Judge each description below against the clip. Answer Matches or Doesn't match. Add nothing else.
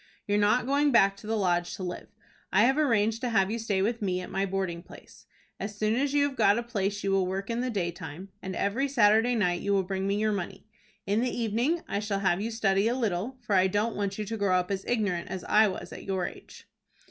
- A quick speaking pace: Matches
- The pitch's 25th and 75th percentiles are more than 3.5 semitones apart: Doesn't match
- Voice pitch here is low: Doesn't match